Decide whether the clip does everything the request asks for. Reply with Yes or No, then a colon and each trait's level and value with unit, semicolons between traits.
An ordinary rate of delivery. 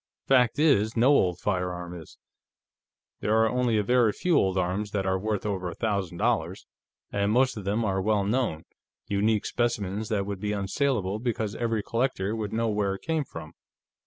Yes: average, 185 wpm